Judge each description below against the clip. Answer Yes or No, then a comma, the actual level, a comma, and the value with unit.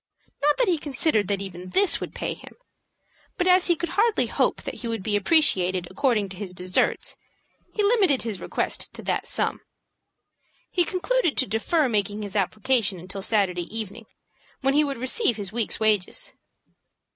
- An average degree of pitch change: No, wide, 8.0 semitones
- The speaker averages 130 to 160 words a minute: No, average, 170 wpm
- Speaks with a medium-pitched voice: No, high, 225 Hz